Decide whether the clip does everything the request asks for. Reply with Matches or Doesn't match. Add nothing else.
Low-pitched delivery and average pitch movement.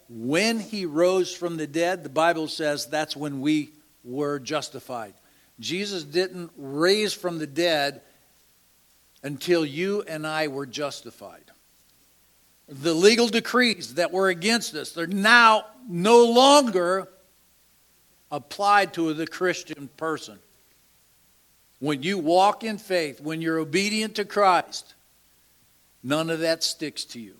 Doesn't match